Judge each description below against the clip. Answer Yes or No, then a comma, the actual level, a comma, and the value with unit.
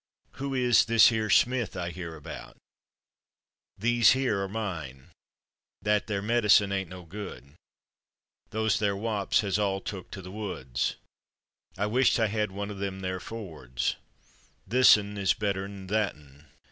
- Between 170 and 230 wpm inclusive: No, average, 145 wpm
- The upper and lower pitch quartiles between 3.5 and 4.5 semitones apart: No, average, 2.9 semitones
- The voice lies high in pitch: No, low, 100 Hz